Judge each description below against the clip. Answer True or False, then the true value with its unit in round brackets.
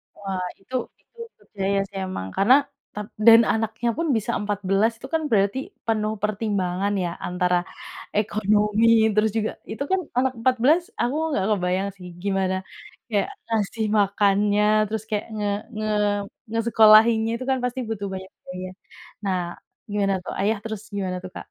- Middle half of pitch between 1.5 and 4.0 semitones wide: True (2.4 semitones)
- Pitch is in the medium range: False (210 Hz)